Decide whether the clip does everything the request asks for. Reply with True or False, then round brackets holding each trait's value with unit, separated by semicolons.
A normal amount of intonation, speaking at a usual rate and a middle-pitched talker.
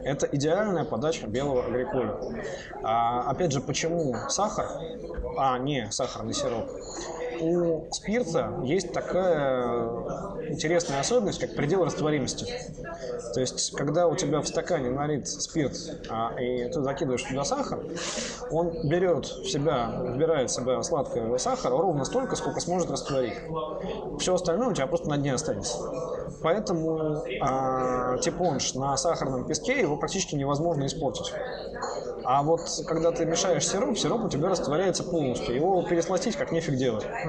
True (4.1 semitones; 140 wpm; 160 Hz)